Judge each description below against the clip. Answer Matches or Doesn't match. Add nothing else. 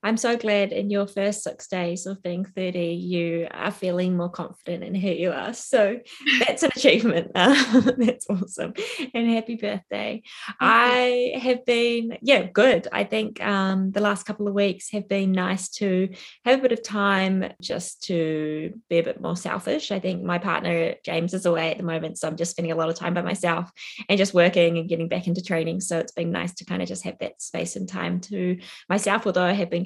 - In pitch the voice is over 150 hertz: Matches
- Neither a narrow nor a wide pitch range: Matches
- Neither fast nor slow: Doesn't match